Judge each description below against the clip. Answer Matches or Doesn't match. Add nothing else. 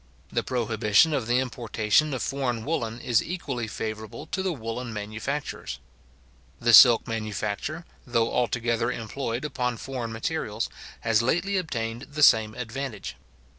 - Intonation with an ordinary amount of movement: Matches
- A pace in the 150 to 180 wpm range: Doesn't match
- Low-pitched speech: Matches